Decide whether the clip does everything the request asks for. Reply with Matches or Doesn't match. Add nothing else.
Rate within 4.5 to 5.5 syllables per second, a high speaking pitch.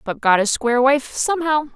Doesn't match